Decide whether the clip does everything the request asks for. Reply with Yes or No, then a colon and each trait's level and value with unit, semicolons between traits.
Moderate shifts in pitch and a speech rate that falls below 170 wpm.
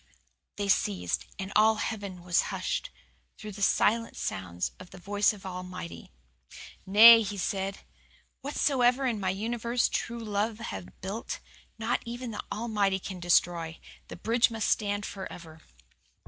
Yes: average, 3.8 semitones; average, 140 wpm